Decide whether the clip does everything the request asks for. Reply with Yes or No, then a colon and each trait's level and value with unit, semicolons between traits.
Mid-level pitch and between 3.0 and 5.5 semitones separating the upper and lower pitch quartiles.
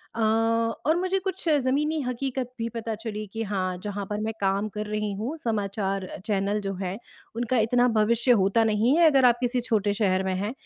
No: high, 220 Hz; average, 3.3 semitones